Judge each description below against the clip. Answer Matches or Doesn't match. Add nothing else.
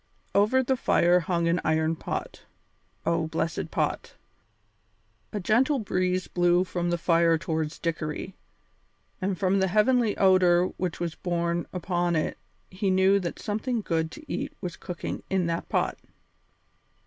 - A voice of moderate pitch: Matches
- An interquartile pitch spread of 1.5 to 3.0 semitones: Matches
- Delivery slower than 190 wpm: Matches